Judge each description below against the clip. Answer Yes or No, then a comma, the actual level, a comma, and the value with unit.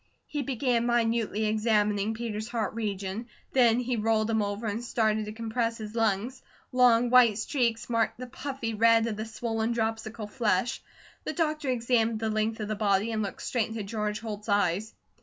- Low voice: No, high, 225 Hz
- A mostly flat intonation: Yes, narrow, 1.7 semitones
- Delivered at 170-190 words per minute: Yes, average, 175 wpm